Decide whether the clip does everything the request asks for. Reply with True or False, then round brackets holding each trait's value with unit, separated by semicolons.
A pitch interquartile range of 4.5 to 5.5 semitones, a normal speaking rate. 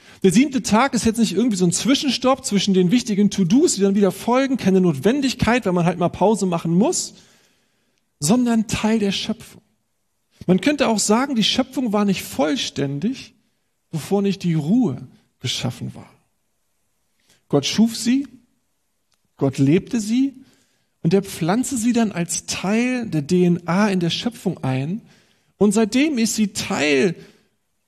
True (5.1 semitones; 150 wpm)